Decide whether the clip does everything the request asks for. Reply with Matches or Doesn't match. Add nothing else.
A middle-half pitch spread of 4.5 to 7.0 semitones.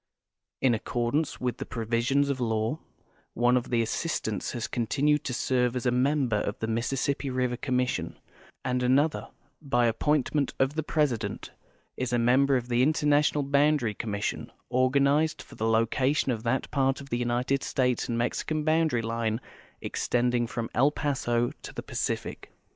Doesn't match